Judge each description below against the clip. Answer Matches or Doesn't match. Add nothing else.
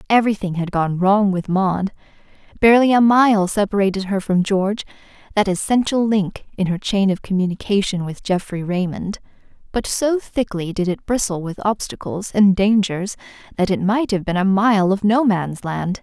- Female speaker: Matches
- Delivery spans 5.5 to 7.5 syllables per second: Doesn't match